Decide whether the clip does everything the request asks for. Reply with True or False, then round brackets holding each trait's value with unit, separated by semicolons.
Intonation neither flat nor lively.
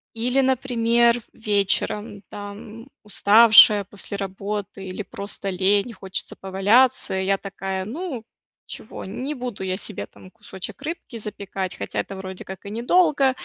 True (3.5 semitones)